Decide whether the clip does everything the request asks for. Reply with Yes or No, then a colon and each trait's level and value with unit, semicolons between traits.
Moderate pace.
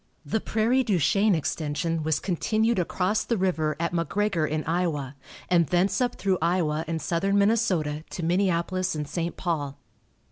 Yes: average, 155 wpm